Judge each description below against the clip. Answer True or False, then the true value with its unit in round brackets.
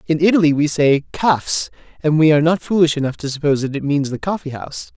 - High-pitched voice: False (155 Hz)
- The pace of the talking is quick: True (240 wpm)